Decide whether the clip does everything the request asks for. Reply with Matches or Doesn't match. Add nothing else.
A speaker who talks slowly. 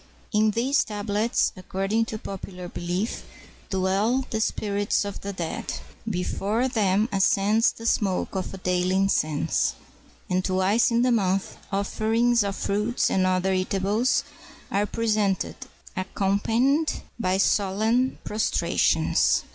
Matches